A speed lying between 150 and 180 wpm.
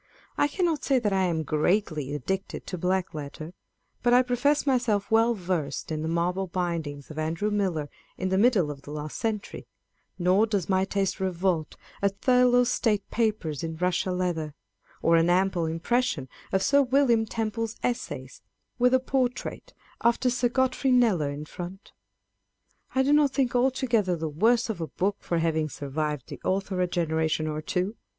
Yes: average, 170 wpm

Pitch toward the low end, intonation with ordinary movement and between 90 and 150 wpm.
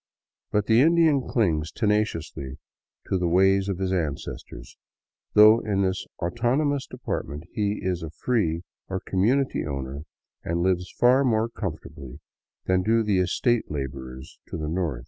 No: very low, 95 Hz; wide, 6.1 semitones; average, 145 wpm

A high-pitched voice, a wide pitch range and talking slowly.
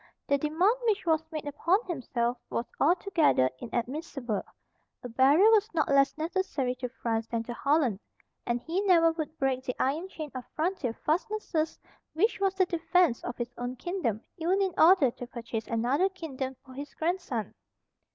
No: very high, 300 Hz; wide, 6.2 semitones; average, 165 wpm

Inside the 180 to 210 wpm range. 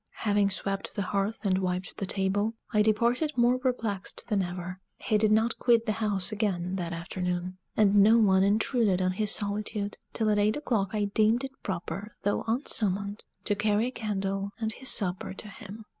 Yes: average, 185 wpm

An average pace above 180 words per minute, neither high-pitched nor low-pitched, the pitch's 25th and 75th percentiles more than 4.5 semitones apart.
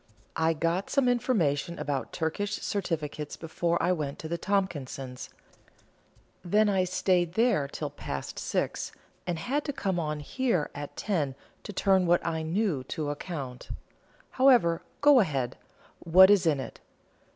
No: average, 145 wpm; medium, 170 Hz; average, 5.1 semitones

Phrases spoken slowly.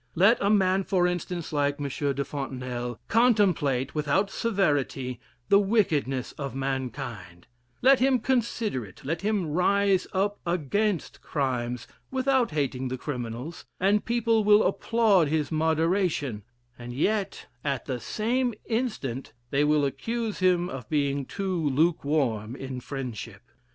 Yes: slow, 130 wpm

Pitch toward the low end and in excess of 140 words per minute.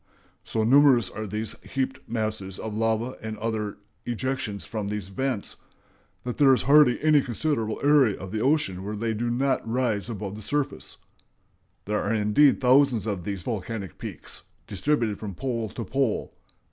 Yes: low, 115 Hz; average, 160 wpm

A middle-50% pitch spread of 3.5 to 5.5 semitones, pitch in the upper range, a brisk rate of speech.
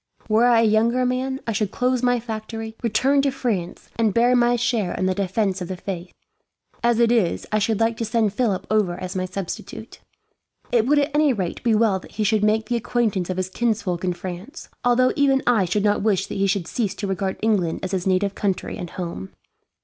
Yes: average, 4.0 semitones; high, 215 Hz; fast, 220 wpm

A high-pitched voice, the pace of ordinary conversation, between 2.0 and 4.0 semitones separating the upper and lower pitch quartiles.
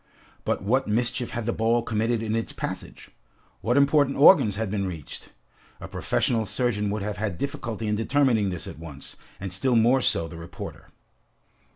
No: low, 110 Hz; average, 175 wpm; average, 3.4 semitones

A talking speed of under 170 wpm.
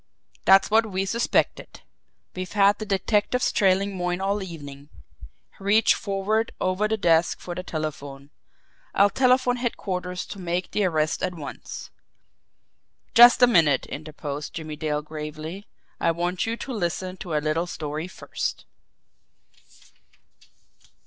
Yes: slow, 135 wpm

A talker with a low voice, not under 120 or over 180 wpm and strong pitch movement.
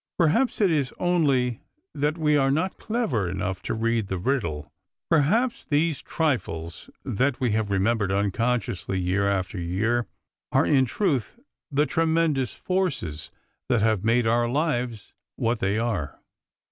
Yes: low, 120 Hz; average, 140 wpm; wide, 7.1 semitones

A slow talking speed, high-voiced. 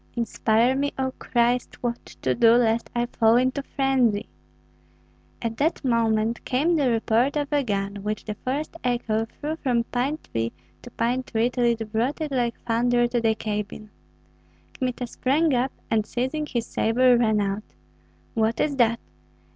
No: average, 165 wpm; high, 240 Hz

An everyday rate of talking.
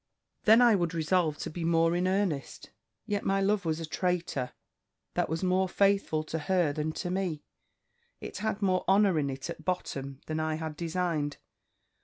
Yes: average, 180 wpm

